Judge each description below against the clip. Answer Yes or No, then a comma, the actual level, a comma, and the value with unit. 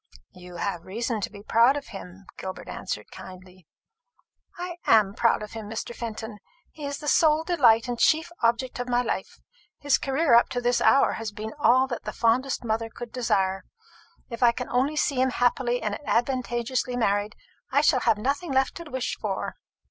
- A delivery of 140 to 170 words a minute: No, average, 185 wpm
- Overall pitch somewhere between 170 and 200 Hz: No, high, 240 Hz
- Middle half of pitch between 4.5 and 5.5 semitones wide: No, average, 3.6 semitones